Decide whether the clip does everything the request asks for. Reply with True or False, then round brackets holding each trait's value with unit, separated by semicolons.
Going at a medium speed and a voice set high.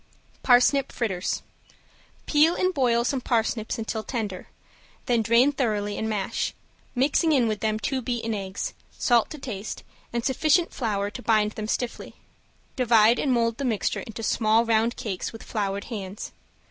True (155 wpm; 230 Hz)